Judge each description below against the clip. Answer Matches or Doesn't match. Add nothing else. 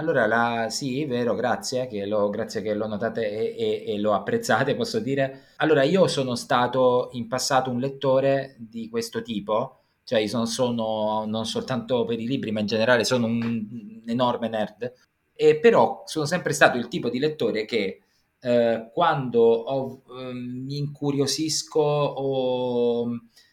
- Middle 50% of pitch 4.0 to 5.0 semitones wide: Matches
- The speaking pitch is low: Matches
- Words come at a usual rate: Matches